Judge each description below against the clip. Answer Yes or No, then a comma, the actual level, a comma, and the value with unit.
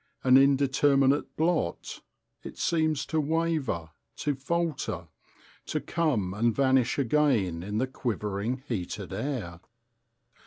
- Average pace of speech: No, slow, 110 wpm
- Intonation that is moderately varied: No, wide, 6.1 semitones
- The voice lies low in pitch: Yes, low, 130 Hz